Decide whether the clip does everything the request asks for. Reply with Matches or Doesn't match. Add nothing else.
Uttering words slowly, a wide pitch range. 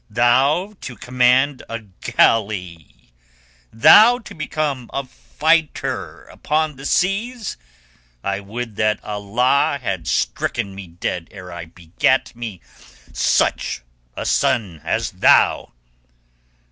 Matches